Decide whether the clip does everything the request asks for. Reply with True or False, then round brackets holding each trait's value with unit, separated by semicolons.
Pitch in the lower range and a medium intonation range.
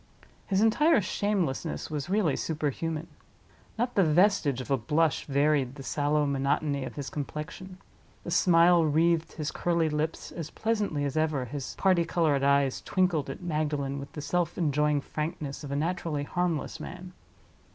False (155 Hz; 3.5 semitones)